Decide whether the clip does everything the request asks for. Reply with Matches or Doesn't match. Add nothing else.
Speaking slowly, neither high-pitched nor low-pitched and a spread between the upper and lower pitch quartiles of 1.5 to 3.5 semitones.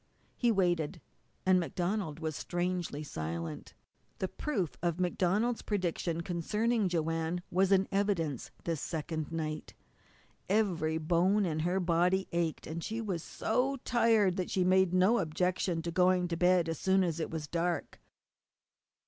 Doesn't match